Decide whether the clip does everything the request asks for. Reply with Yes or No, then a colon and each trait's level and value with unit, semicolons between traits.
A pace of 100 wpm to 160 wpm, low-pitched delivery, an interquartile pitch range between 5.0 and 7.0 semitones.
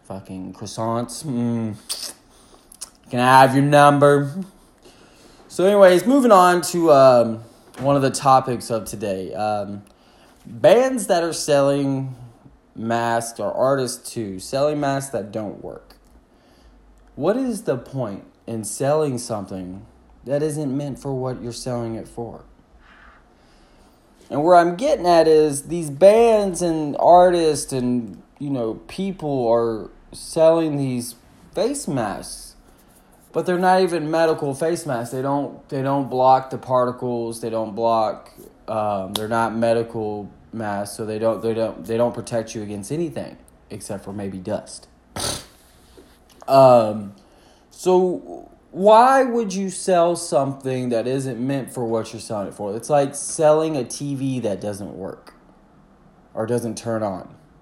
Yes: average, 140 wpm; low, 130 Hz; average, 5.3 semitones